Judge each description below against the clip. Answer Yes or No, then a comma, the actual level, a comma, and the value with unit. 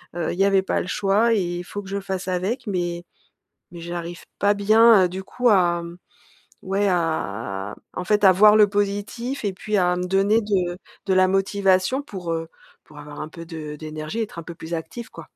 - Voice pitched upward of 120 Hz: Yes, medium, 185 Hz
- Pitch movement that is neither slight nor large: Yes, average, 3.0 semitones